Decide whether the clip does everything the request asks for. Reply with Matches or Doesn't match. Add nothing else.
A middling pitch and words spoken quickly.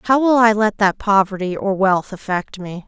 Doesn't match